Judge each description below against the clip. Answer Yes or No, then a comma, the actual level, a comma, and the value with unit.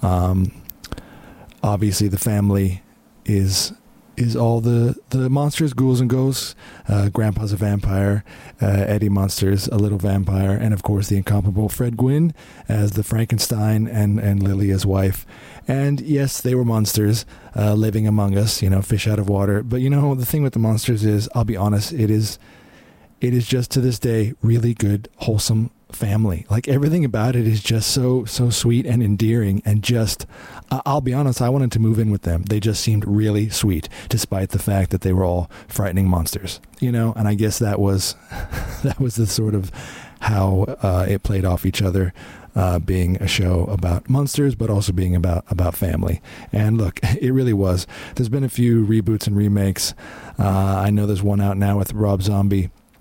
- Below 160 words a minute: No, average, 190 wpm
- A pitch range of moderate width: Yes, average, 3.1 semitones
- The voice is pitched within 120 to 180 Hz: No, low, 105 Hz